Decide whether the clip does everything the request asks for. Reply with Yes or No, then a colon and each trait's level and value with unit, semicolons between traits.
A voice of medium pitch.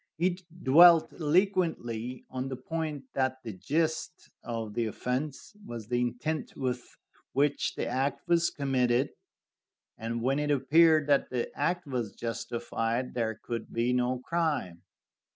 No: low, 130 Hz